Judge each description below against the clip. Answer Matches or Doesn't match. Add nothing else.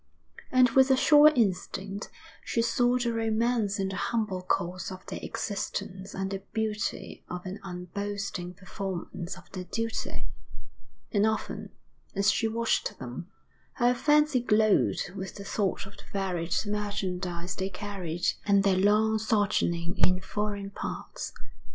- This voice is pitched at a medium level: Doesn't match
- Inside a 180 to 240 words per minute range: Doesn't match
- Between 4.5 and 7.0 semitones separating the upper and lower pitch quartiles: Doesn't match